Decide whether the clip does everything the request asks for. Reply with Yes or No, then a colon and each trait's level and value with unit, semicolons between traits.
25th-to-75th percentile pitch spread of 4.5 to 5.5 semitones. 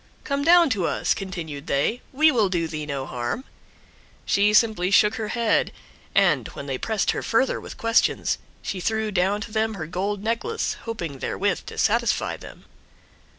Yes: average, 5.1 semitones